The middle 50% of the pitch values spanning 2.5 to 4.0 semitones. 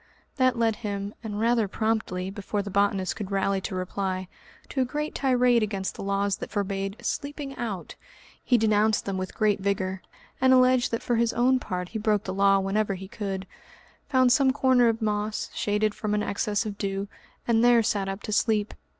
Yes: average, 3.1 semitones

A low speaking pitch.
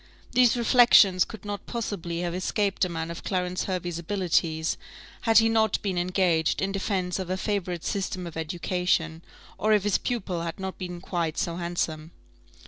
No: medium, 185 Hz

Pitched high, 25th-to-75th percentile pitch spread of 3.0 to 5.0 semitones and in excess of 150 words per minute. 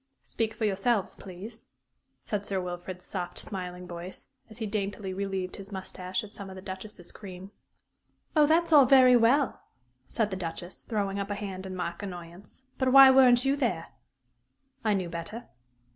Yes: high, 200 Hz; average, 3.6 semitones; average, 170 wpm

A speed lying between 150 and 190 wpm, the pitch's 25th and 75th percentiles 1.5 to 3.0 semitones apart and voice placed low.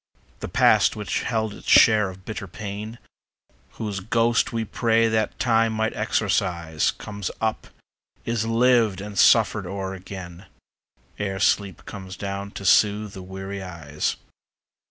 No: slow, 135 wpm; average, 2.7 semitones; low, 100 Hz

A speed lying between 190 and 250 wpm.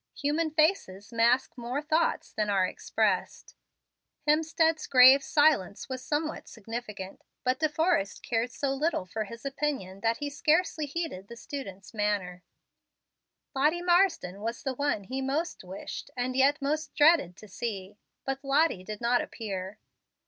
No: average, 145 wpm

